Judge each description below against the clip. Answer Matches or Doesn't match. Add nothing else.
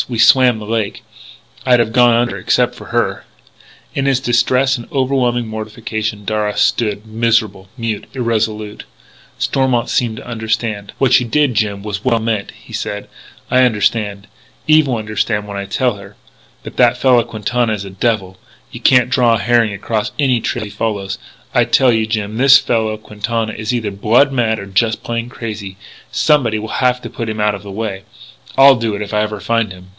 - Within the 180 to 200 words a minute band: Matches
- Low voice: Matches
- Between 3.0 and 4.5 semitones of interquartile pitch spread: Doesn't match